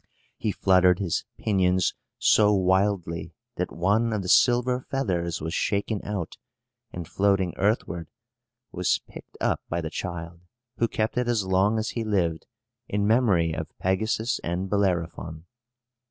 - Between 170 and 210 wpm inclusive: No, average, 140 wpm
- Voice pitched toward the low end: Yes, very low, 95 Hz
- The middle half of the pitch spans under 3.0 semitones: No, average, 3.8 semitones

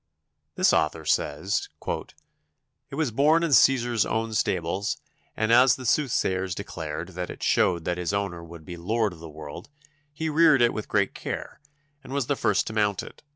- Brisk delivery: No, average, 180 wpm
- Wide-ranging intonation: Yes, wide, 6.6 semitones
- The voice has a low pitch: Yes, low, 105 Hz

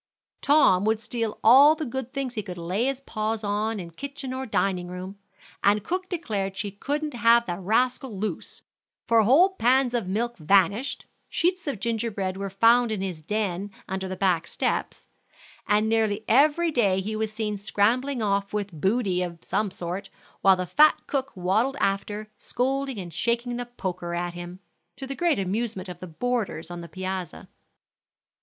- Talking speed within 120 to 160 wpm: No, average, 175 wpm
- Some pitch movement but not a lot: Yes, average, 4.6 semitones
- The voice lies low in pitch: No, high, 215 Hz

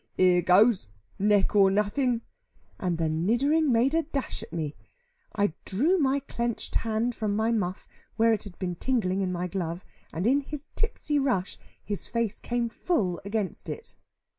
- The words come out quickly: No, average, 165 wpm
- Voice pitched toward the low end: No, high, 215 Hz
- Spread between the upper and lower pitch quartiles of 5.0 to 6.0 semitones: Yes, average, 5.3 semitones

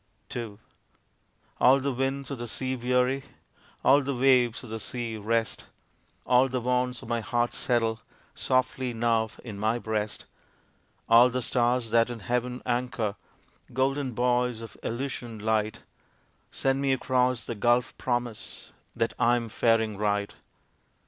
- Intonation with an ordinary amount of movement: No, narrow, 1.9 semitones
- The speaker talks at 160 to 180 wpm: No, average, 140 wpm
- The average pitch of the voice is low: Yes, low, 120 Hz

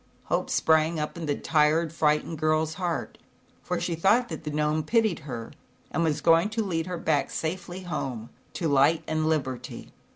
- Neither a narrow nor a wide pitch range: No, narrow, 2.2 semitones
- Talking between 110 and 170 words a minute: No, average, 185 wpm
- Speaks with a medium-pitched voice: Yes, medium, 160 Hz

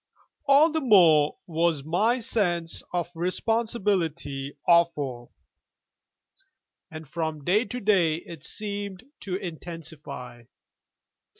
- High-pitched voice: No, medium, 170 Hz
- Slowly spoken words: Yes, slow, 95 wpm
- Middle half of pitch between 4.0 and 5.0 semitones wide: Yes, average, 4.5 semitones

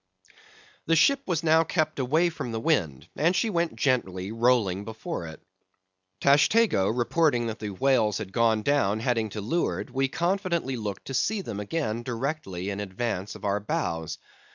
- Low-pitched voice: Yes, low, 120 Hz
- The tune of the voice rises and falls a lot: Yes, wide, 7.4 semitones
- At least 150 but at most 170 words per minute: Yes, average, 165 wpm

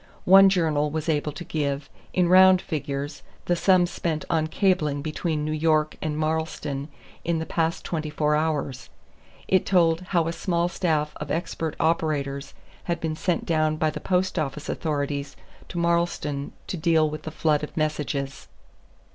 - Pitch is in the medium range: Yes, medium, 155 Hz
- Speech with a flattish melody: Yes, narrow, 2.2 semitones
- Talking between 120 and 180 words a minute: Yes, average, 165 wpm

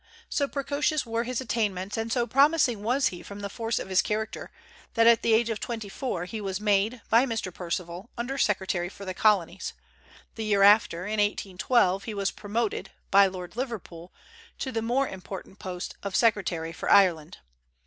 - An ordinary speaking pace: Yes, average, 180 wpm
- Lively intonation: No, average, 3.6 semitones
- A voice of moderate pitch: No, high, 210 Hz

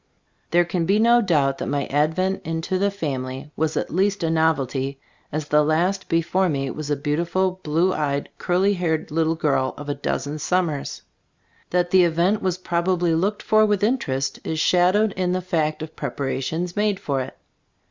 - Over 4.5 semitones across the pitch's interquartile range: No, average, 4.0 semitones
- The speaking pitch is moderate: Yes, medium, 165 Hz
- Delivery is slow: No, average, 180 wpm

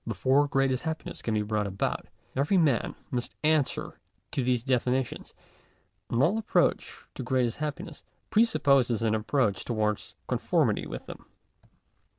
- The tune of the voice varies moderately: Yes, average, 4.1 semitones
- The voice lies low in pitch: Yes, low, 130 Hz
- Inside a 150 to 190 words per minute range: No, slow, 135 wpm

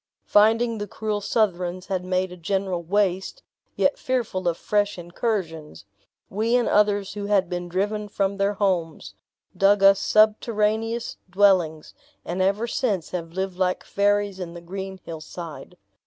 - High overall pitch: Yes, high, 195 Hz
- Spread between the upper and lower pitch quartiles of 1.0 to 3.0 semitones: Yes, narrow, 2.6 semitones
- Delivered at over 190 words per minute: No, average, 145 wpm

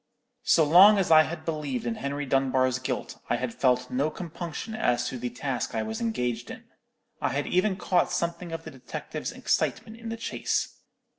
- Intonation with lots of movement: Yes, wide, 5.8 semitones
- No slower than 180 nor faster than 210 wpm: Yes, average, 190 wpm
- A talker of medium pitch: Yes, medium, 145 Hz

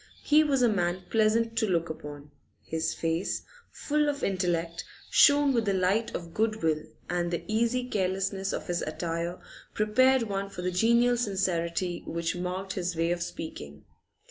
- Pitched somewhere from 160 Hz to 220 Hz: Yes, high, 190 Hz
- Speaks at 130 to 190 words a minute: Yes, average, 165 wpm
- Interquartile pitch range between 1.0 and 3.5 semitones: No, average, 4.9 semitones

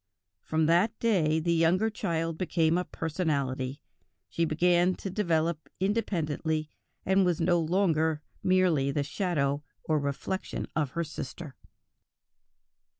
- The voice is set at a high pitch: No, medium, 165 Hz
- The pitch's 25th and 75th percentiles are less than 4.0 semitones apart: Yes, average, 2.9 semitones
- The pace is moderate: No, slow, 120 wpm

